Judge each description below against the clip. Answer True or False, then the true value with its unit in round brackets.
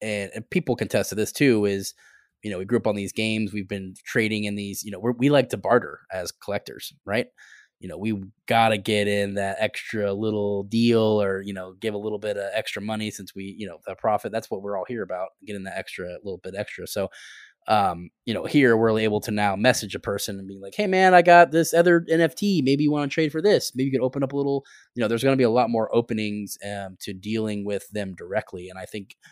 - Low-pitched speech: True (105 Hz)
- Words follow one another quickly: True (250 wpm)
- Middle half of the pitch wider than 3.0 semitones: True (3.6 semitones)